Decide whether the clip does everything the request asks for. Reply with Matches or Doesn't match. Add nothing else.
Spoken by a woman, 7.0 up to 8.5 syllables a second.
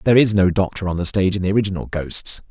Doesn't match